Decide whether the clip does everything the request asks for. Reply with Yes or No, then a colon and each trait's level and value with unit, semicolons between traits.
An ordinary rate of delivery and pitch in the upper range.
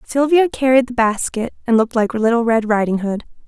Yes: average, 190 wpm; high, 235 Hz